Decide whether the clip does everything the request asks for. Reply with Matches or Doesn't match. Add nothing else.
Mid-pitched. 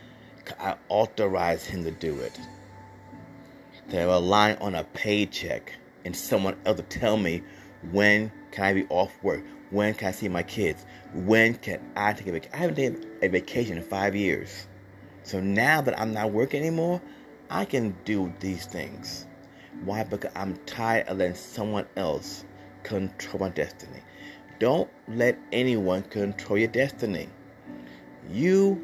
Doesn't match